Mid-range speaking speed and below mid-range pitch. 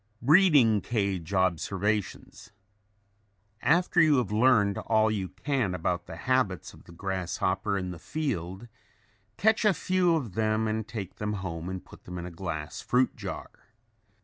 Yes: average, 150 wpm; low, 105 Hz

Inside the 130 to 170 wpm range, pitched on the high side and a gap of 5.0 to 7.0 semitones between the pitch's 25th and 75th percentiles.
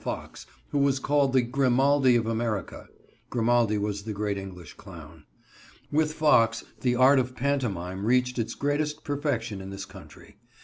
No: average, 150 wpm; low, 120 Hz; average, 5.3 semitones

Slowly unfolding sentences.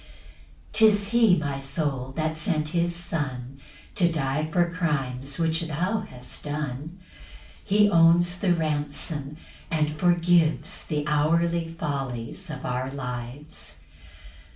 Yes: slow, 120 wpm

